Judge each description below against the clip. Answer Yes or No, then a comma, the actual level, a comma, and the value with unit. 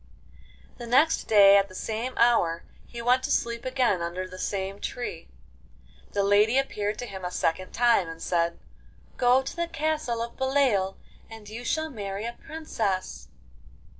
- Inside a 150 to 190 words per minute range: Yes, average, 165 wpm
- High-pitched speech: Yes, high, 225 Hz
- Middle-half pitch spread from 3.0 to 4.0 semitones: No, average, 4.5 semitones